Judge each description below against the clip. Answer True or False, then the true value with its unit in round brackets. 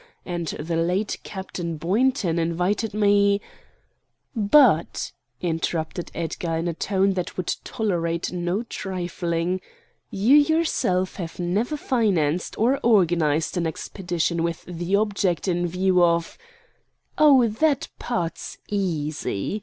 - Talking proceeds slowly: True (115 wpm)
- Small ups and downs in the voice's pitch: False (3.7 semitones)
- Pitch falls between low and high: True (180 Hz)